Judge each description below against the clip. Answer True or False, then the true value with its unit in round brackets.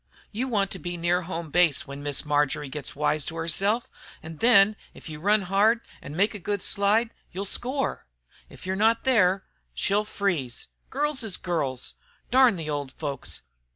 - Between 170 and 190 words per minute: True (175 wpm)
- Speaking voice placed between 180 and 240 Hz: True (185 Hz)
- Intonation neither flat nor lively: False (5.7 semitones)